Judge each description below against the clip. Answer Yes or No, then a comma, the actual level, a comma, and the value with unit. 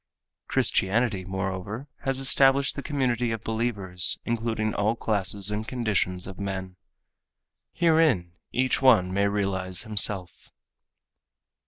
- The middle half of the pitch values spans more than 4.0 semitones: Yes, average, 4.4 semitones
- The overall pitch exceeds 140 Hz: No, low, 105 Hz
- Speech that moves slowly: Yes, slow, 110 wpm